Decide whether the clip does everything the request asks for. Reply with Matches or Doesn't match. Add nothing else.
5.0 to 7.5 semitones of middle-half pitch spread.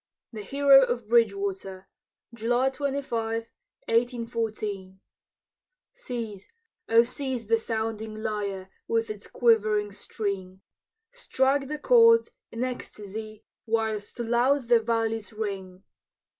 Doesn't match